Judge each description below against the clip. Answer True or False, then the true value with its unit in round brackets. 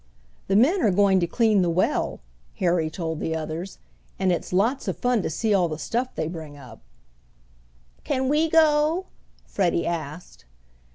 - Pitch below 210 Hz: True (185 Hz)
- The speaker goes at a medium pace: True (165 wpm)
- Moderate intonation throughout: False (7.1 semitones)